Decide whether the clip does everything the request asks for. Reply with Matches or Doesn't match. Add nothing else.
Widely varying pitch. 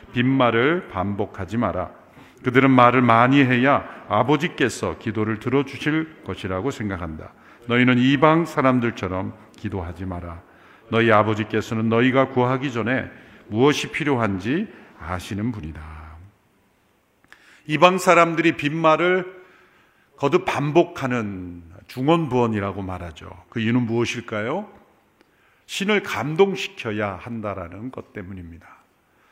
Matches